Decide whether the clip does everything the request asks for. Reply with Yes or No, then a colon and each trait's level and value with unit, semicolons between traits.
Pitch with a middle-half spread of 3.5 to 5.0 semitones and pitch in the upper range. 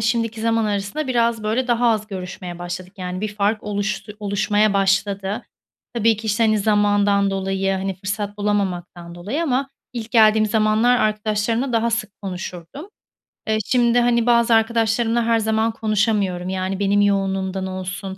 No: average, 2.7 semitones; high, 210 Hz